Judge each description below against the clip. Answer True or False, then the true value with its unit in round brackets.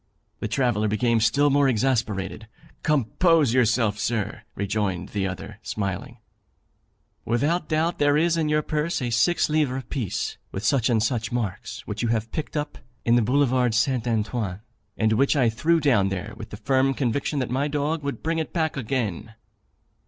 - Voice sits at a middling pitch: False (125 Hz)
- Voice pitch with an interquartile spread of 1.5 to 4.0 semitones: False (4.9 semitones)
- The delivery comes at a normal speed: True (170 wpm)